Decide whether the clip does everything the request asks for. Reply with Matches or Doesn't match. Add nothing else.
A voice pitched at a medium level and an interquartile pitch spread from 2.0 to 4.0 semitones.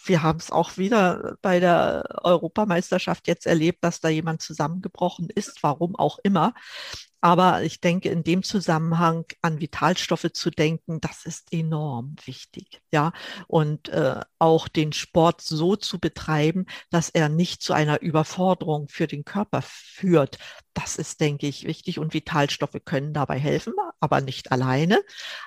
Matches